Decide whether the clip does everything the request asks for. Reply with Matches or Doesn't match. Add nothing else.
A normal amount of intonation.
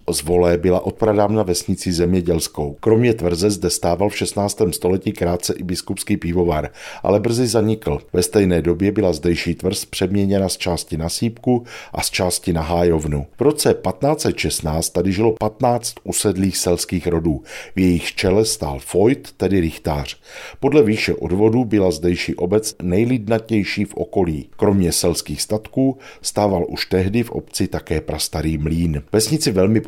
Matches